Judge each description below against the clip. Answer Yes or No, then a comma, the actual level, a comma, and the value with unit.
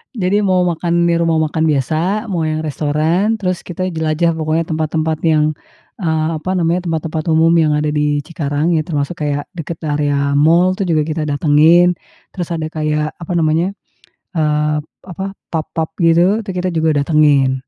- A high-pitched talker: No, medium, 160 Hz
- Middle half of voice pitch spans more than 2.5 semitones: No, narrow, 2.2 semitones